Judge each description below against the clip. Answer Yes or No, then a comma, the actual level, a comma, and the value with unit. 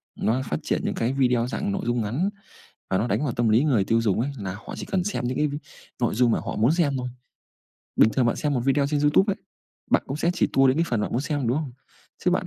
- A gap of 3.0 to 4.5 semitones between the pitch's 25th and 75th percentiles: Yes, average, 4.1 semitones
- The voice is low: Yes, low, 130 Hz